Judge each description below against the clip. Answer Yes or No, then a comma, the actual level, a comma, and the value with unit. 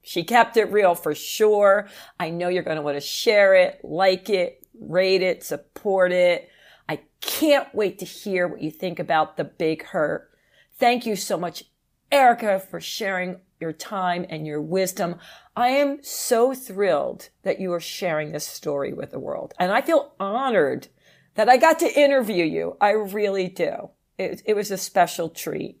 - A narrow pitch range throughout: No, average, 4.1 semitones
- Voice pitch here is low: No, high, 190 Hz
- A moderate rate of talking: Yes, average, 180 wpm